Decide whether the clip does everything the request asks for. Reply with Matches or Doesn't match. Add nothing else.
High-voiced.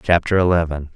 Doesn't match